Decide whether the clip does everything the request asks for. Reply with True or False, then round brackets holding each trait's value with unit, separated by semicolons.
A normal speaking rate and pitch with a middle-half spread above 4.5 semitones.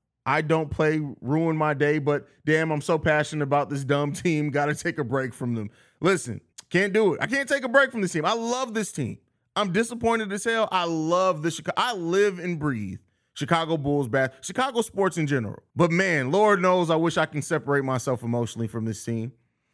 False (215 wpm; 5.1 semitones)